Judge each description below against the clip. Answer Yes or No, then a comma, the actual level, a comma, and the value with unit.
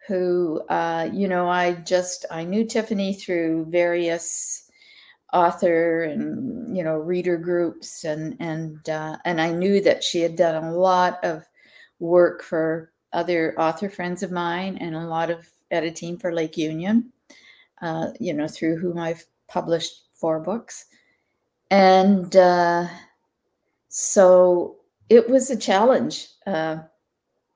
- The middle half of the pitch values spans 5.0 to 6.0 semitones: No, narrow, 2.5 semitones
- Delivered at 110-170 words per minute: Yes, slow, 135 wpm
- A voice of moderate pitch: Yes, medium, 175 Hz